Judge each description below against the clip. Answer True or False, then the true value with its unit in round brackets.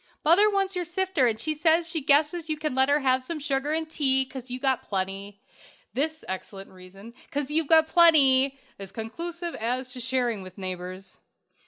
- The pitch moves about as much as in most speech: False (5.8 semitones)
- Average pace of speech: True (185 wpm)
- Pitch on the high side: True (270 Hz)